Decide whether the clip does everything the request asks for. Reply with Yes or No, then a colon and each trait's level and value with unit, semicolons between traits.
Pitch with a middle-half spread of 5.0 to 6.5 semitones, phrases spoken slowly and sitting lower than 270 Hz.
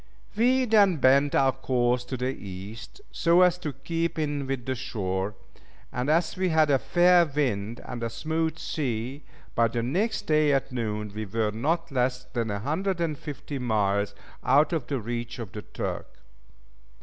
No: wide, 5.6 semitones; average, 165 wpm; low, 135 Hz